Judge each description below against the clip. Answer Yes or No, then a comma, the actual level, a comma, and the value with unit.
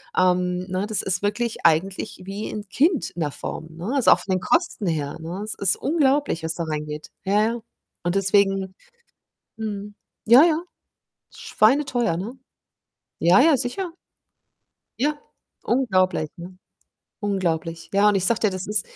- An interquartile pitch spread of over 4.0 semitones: Yes, average, 4.7 semitones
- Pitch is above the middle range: Yes, high, 200 Hz